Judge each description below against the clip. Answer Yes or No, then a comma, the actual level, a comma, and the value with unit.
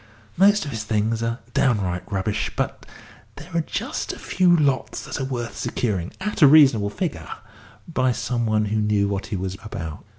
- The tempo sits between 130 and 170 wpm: No, average, 185 wpm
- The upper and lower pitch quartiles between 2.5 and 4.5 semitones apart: No, average, 5.2 semitones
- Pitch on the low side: Yes, low, 115 Hz